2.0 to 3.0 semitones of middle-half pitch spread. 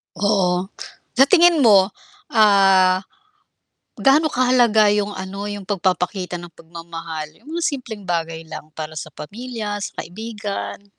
No: average, 4.2 semitones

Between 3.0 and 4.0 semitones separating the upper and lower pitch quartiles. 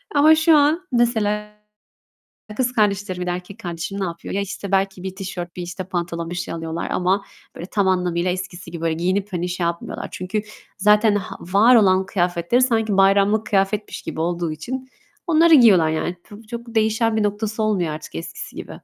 Yes: average, 3.6 semitones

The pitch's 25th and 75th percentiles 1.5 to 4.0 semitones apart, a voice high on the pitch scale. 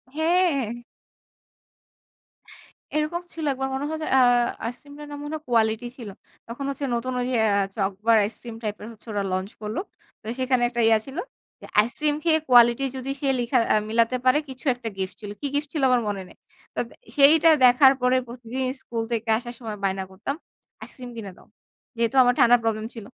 Yes: average, 3.7 semitones; high, 245 Hz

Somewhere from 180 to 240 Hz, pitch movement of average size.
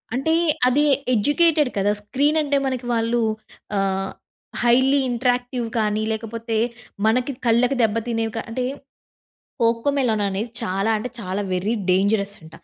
Yes: high, 230 Hz; average, 3.4 semitones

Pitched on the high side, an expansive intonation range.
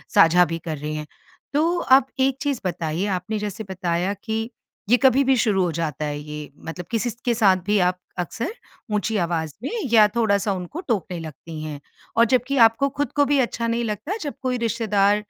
Yes: high, 210 Hz; wide, 6.0 semitones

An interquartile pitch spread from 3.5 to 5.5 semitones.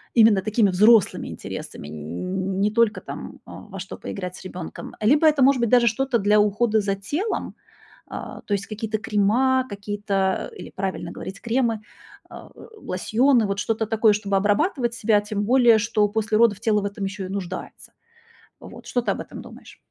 No: average, 2.9 semitones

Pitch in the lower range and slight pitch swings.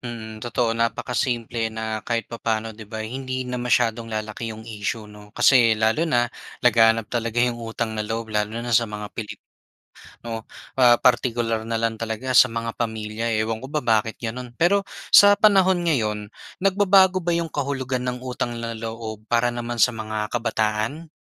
Yes: low, 115 Hz; narrow, 2.1 semitones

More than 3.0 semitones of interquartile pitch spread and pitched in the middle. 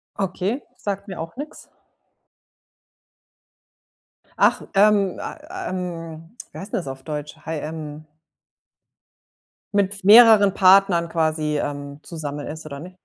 Yes: average, 4.4 semitones; medium, 170 Hz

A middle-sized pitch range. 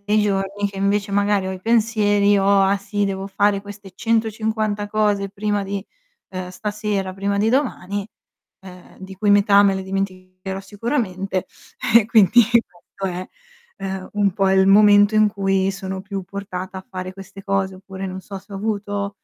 No: narrow, 1.3 semitones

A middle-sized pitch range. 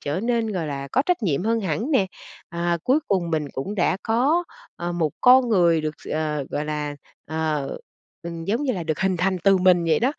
No: wide, 6.0 semitones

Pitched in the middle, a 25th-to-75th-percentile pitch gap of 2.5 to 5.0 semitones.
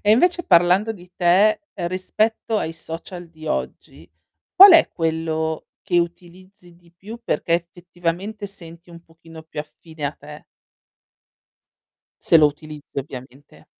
Yes: medium, 170 Hz; average, 2.9 semitones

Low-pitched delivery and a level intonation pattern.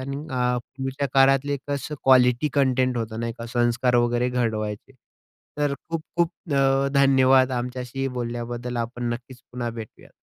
Yes: low, 125 Hz; narrow, 2.1 semitones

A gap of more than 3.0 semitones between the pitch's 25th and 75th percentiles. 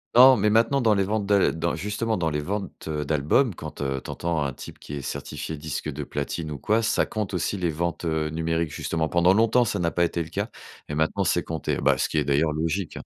Yes: average, 4.7 semitones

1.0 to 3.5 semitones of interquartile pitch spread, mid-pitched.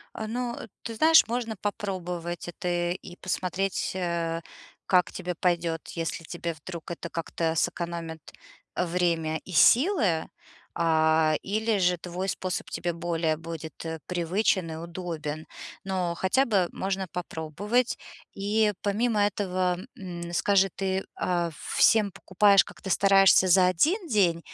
Yes: average, 2.9 semitones; medium, 180 Hz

